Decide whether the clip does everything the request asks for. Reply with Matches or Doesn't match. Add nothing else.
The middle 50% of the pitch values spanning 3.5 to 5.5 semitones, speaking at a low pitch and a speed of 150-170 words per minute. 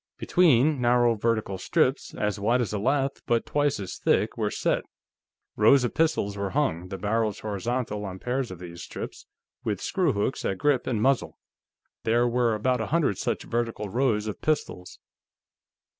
Matches